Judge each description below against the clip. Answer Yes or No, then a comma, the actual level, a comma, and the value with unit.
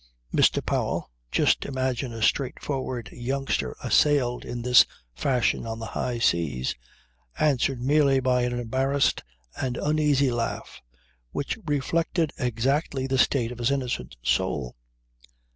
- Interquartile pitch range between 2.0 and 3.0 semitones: Yes, average, 2.7 semitones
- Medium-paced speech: No, slow, 125 wpm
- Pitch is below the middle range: Yes, low, 125 Hz